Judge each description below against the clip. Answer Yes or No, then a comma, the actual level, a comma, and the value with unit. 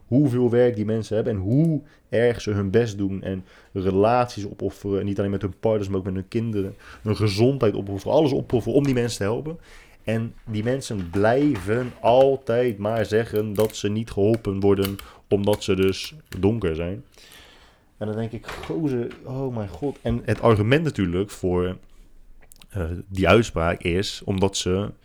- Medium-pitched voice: No, low, 105 Hz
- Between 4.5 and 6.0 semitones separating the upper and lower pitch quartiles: No, average, 3.4 semitones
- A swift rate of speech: No, average, 175 wpm